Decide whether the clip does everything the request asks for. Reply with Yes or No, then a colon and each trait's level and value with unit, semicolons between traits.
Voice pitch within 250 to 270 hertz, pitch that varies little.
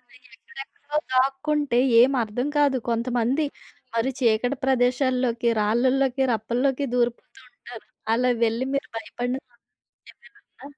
Yes: very high, 255 Hz; narrow, 2.3 semitones